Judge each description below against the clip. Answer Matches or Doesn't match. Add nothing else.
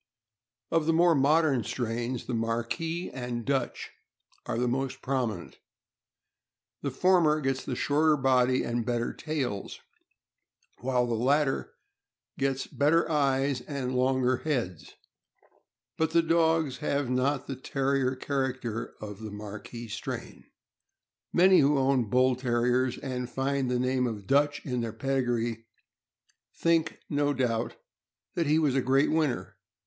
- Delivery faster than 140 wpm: Doesn't match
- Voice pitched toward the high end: Doesn't match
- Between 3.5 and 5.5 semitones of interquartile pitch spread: Doesn't match